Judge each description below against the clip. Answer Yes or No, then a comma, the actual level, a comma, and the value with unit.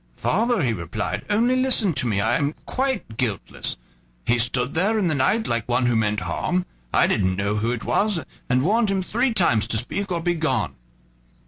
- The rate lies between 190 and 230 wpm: Yes, average, 195 wpm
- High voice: No, low, 135 Hz